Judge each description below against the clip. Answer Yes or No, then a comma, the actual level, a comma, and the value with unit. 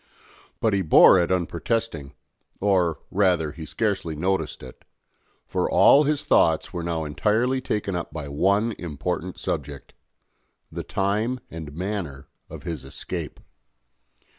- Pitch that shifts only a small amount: No, average, 4.7 semitones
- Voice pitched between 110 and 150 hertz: No, very low, 90 Hz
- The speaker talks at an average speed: No, slow, 130 wpm